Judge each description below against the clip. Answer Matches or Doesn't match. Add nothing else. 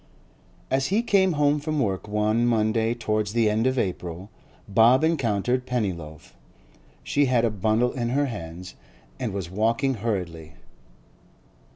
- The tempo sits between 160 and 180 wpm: Doesn't match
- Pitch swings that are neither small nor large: Matches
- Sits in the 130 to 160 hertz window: Doesn't match